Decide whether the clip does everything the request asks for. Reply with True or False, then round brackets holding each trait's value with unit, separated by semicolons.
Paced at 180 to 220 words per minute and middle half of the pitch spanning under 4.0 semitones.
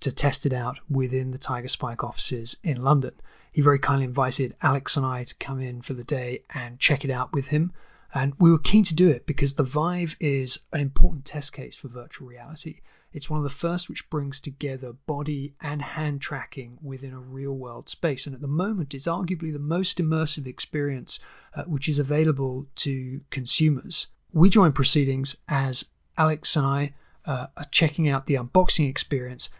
True (190 wpm; 2.7 semitones)